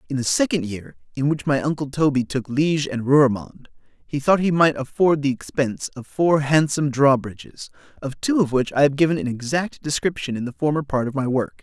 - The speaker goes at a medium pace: No, fast, 215 wpm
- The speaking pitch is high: No, medium, 140 Hz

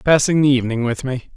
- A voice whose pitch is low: Yes, low, 130 Hz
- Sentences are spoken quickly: Yes, fast, 220 wpm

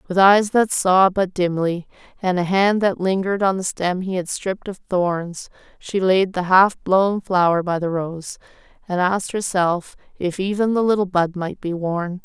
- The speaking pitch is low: No, medium, 185 Hz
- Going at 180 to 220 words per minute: Yes, average, 190 wpm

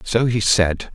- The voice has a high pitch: No, low, 105 Hz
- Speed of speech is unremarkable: Yes, average, 190 wpm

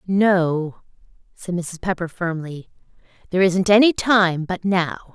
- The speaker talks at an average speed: No, slow, 130 wpm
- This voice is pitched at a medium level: Yes, medium, 180 Hz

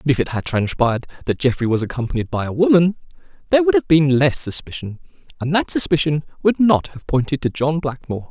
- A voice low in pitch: No, medium, 145 Hz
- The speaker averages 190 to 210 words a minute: Yes, average, 200 wpm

